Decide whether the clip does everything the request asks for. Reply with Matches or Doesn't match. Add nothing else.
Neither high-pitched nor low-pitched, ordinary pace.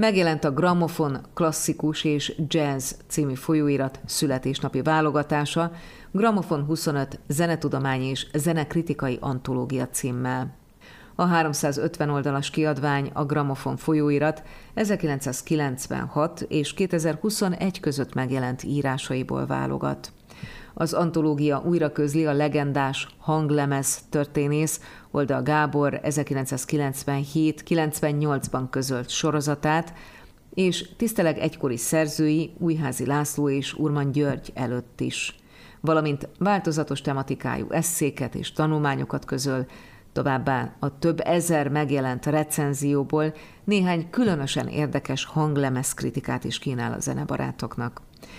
Doesn't match